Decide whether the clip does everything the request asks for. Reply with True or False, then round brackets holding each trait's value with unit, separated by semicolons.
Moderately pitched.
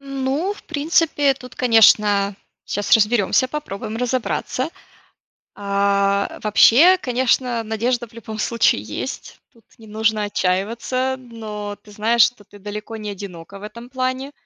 False (225 Hz)